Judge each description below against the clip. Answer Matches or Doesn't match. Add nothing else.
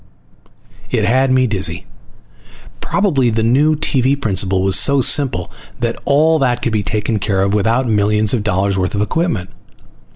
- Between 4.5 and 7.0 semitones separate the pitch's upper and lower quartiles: Matches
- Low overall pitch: Matches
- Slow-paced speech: Doesn't match